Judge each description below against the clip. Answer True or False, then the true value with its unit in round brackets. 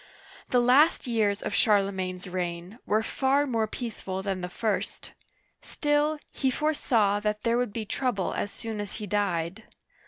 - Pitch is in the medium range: False (215 Hz)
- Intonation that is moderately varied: True (4.1 semitones)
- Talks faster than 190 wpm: False (155 wpm)